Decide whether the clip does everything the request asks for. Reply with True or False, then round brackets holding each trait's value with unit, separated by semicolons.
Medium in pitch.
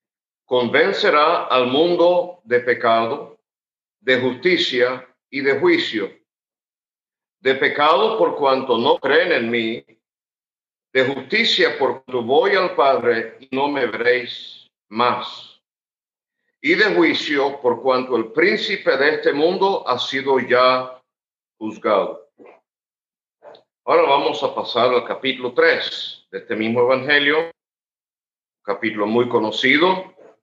False (130 Hz)